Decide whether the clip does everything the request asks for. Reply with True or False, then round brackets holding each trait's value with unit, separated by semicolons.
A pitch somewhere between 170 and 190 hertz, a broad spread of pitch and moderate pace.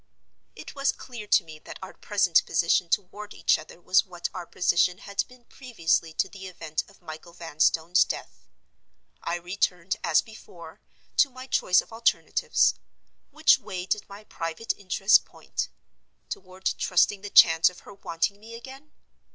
False (185 Hz; 3.8 semitones; 160 wpm)